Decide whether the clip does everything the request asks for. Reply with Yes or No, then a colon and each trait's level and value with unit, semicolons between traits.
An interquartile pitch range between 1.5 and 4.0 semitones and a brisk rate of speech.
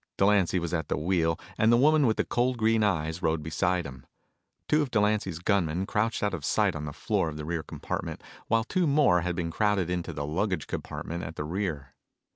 No: average, 5.0 semitones; fast, 215 wpm